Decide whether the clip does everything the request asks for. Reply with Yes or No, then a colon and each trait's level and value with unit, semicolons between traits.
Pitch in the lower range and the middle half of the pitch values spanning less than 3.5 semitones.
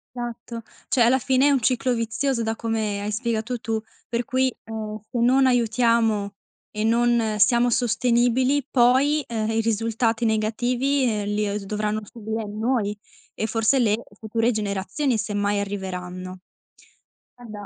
No: high, 225 Hz; narrow, 2.5 semitones